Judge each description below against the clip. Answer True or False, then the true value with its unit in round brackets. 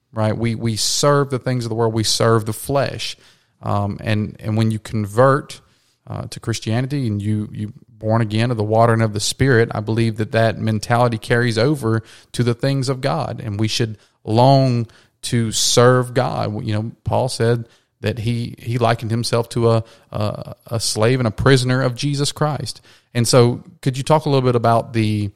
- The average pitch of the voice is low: True (115 Hz)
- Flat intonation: True (2.3 semitones)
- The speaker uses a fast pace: False (195 wpm)